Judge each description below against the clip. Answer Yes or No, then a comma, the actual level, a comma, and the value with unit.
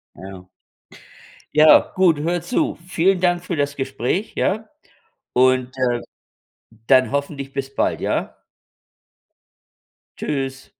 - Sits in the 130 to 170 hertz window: Yes, medium, 140 Hz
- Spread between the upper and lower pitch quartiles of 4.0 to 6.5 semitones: Yes, average, 5.3 semitones